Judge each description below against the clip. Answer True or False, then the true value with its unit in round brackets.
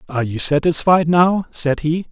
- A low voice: False (160 Hz)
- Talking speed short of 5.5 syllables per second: True (4.8 syllables/s)